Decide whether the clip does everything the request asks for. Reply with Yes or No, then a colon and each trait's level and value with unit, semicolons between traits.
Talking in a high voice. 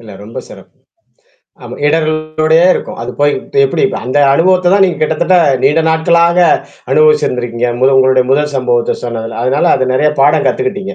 No: medium, 150 Hz